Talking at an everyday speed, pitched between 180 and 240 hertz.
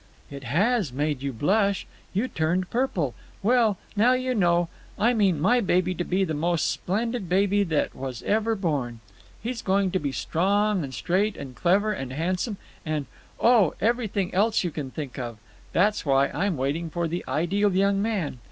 Yes: average, 170 wpm; medium, 185 Hz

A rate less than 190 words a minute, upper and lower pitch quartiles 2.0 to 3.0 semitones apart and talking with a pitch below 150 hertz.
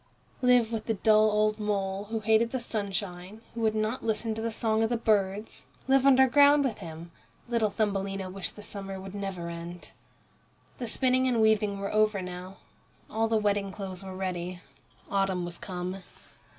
No: average, 175 wpm; average, 2.7 semitones; high, 210 Hz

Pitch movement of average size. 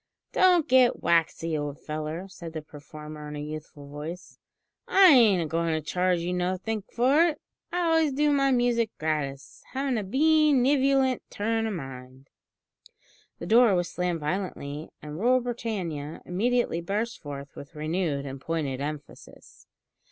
No: wide, 8.2 semitones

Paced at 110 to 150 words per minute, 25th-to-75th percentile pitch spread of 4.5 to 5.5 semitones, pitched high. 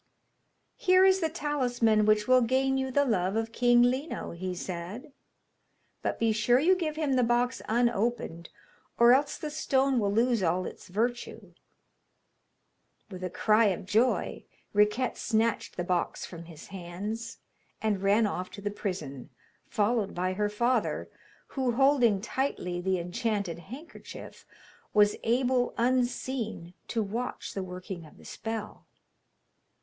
Yes: average, 145 wpm; average, 4.8 semitones; high, 225 Hz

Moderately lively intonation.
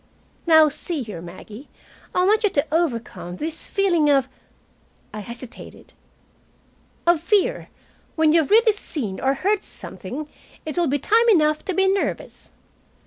No: wide, 6.3 semitones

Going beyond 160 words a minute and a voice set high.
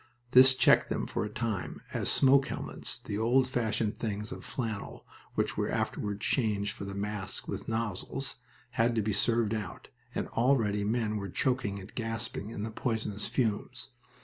No: average, 170 wpm; low, 110 Hz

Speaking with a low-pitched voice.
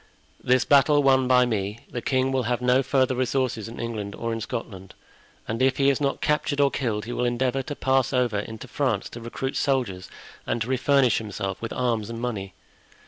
Yes: low, 125 Hz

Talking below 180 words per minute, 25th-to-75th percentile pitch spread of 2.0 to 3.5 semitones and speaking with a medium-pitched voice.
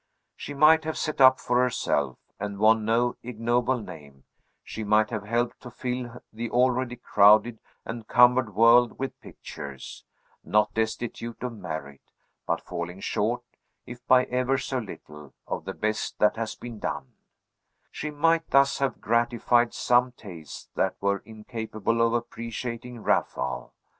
No: average, 145 wpm; average, 2.8 semitones; low, 115 Hz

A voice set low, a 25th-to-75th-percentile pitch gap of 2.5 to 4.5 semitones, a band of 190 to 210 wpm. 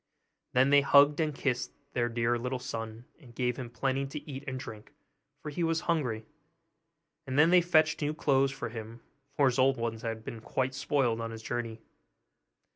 Yes: low, 130 Hz; average, 3.5 semitones; average, 195 wpm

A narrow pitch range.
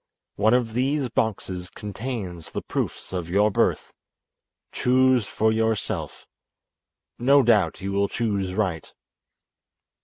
No: average, 4.2 semitones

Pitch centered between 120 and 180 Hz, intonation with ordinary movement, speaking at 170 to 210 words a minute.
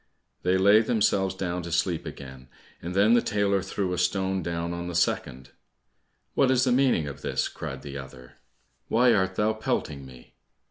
No: very low, 95 Hz; average, 3.8 semitones; average, 180 wpm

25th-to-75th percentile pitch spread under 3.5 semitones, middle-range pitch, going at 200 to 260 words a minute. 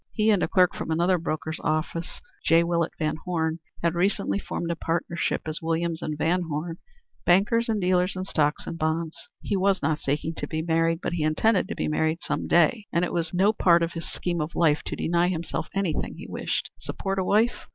Yes: narrow, 2.4 semitones; medium, 170 Hz; fast, 205 wpm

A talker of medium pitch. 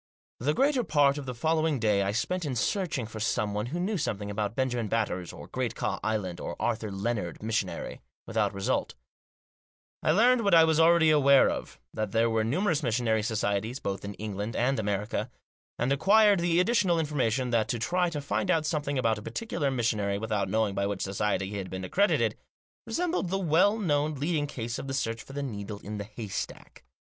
No: low, 120 Hz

